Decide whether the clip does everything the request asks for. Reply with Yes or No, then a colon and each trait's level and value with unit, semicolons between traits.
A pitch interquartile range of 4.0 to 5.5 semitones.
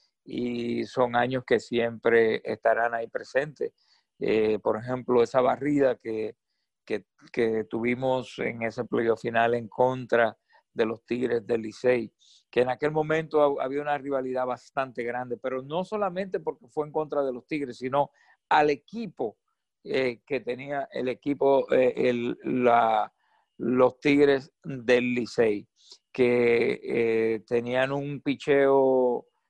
No: average, 3.1 semitones